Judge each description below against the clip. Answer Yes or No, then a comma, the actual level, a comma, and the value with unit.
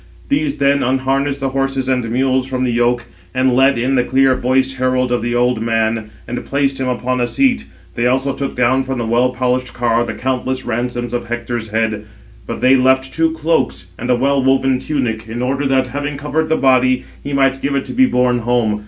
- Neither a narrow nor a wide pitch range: No, narrow, 1.8 semitones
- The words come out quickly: Yes, fast, 215 wpm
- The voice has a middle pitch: No, low, 130 Hz